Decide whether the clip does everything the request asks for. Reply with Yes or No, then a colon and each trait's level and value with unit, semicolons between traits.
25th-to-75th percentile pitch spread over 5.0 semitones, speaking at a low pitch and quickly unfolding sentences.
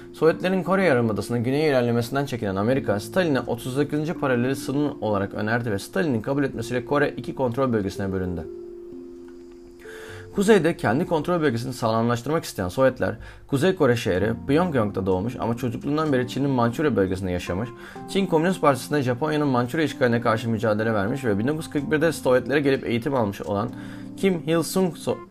Yes: wide, 5.5 semitones; low, 130 Hz; fast, 145 wpm